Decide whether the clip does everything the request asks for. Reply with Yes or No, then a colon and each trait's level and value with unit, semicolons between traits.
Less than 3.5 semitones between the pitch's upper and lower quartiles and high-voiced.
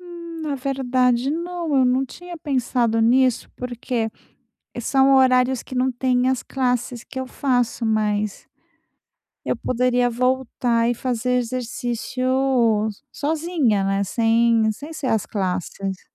Yes: narrow, 2.5 semitones; very high, 250 Hz